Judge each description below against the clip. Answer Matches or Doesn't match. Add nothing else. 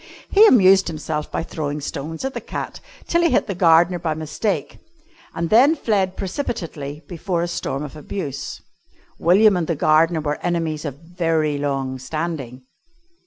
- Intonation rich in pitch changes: Doesn't match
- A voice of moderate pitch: Matches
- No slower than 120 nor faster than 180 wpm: Matches